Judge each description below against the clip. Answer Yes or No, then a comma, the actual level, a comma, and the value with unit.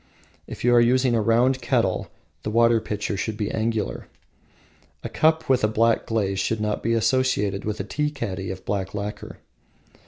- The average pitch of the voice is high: No, low, 110 Hz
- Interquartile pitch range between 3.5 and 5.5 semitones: No, average, 2.8 semitones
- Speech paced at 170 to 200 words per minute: Yes, average, 180 wpm